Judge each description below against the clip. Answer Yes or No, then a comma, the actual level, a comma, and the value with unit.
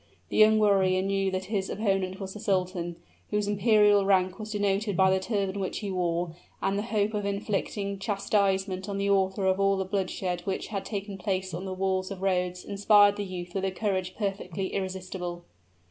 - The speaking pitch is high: Yes, high, 195 Hz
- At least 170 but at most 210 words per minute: Yes, average, 190 wpm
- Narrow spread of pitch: Yes, narrow, 1.4 semitones